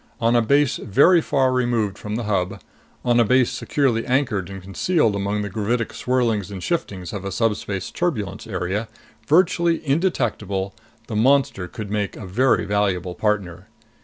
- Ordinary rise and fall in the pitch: Yes, average, 4.5 semitones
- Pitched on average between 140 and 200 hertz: No, low, 110 Hz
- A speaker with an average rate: Yes, average, 160 wpm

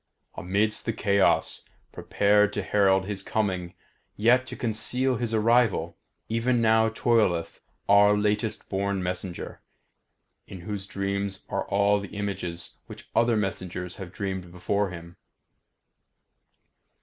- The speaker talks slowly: Yes, slow, 120 wpm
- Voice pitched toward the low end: Yes, low, 100 Hz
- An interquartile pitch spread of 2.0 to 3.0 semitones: Yes, narrow, 2.5 semitones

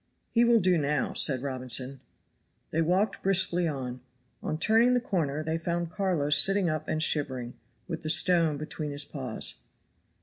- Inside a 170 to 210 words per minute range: No, average, 160 wpm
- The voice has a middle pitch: Yes, medium, 155 Hz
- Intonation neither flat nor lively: Yes, average, 4.3 semitones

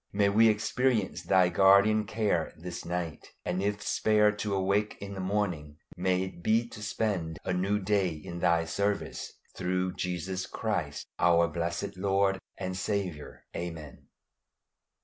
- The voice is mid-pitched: No, very low, 95 Hz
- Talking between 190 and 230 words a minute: No, average, 145 wpm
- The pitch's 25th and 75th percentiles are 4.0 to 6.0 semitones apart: No, average, 2.9 semitones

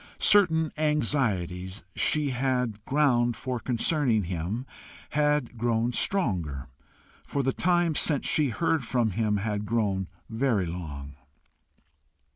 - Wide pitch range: Yes, wide, 6.6 semitones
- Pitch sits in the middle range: No, low, 120 Hz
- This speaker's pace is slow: Yes, slow, 110 wpm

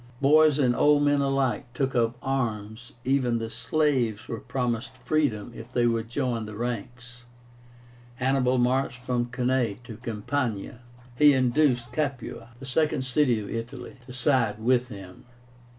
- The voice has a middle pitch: No, low, 125 Hz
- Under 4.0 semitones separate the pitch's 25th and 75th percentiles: Yes, average, 2.7 semitones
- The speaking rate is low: No, average, 145 wpm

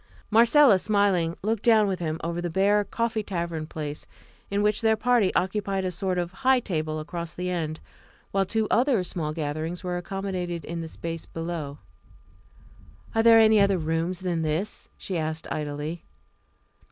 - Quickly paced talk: No, average, 165 wpm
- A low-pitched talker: No, medium, 180 Hz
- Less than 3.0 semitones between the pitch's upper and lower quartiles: No, average, 4.2 semitones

